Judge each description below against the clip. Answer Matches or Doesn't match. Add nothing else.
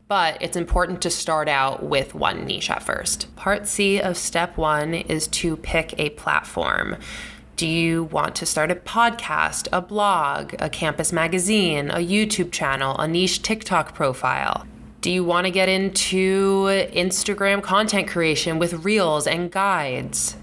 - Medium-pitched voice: Matches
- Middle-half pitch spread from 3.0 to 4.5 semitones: Matches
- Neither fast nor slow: Matches